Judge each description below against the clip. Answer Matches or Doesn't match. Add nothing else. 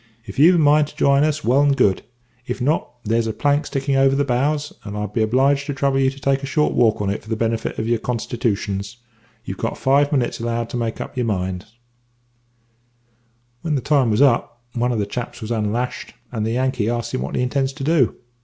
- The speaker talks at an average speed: Doesn't match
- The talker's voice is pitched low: Matches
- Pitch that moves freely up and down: Doesn't match